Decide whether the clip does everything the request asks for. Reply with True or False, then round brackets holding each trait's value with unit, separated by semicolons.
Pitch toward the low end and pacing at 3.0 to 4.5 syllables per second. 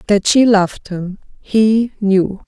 False (205 Hz; 3.5 syllables/s)